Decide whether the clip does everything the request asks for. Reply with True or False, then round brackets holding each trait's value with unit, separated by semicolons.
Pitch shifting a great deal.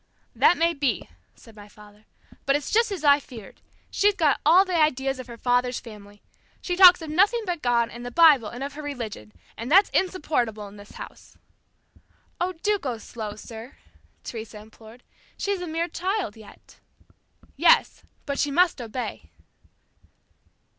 True (7.4 semitones)